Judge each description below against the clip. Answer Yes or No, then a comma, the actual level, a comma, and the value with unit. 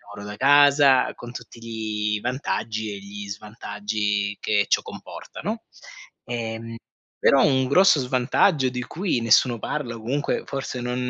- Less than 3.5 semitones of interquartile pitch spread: No, average, 3.9 semitones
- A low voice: Yes, low, 120 Hz